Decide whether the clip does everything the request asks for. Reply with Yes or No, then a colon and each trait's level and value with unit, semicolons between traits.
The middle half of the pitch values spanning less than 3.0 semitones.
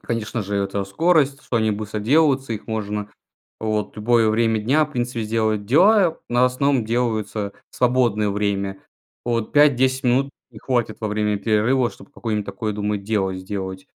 No: average, 3.4 semitones